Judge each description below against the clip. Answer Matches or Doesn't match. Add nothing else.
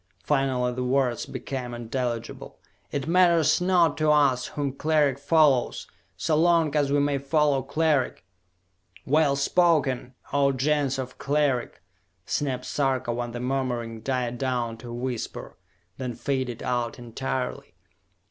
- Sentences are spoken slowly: Matches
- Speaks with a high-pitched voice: Doesn't match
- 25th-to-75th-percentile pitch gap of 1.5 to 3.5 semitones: Matches